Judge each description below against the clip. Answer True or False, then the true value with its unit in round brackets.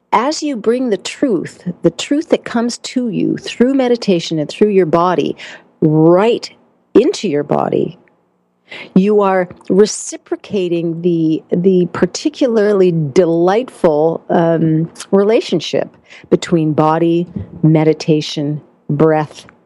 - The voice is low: False (180 Hz)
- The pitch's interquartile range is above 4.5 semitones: True (5.0 semitones)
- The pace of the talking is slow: True (105 wpm)